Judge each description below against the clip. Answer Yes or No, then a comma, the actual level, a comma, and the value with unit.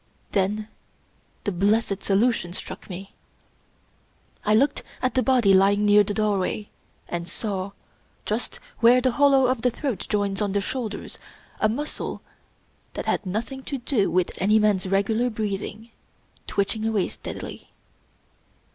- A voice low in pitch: No, high, 210 Hz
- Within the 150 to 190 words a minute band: No, average, 140 wpm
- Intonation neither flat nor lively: Yes, average, 3.2 semitones